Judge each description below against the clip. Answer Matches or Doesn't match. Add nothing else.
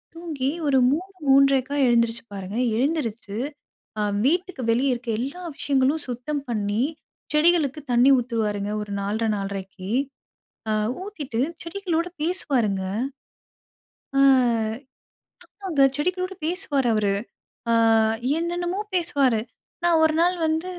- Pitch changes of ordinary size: Doesn't match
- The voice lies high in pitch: Matches